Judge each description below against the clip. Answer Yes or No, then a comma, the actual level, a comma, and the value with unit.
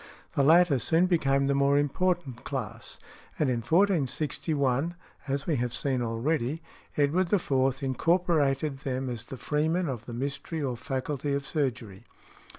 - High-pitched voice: No, medium, 140 Hz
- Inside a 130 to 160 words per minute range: Yes, average, 145 wpm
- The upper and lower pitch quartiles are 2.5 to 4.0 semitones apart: Yes, average, 3.7 semitones